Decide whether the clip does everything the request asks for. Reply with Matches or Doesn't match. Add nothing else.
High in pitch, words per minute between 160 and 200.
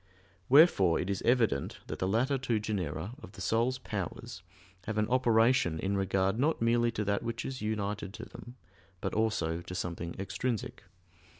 Doesn't match